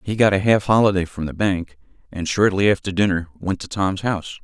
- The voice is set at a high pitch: No, very low, 95 Hz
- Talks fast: Yes, fast, 215 wpm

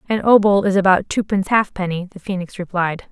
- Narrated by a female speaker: Yes, female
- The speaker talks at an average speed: Yes, average, 175 wpm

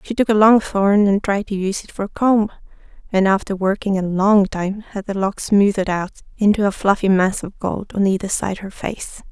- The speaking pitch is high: Yes, high, 200 Hz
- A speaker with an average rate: No, fast, 225 wpm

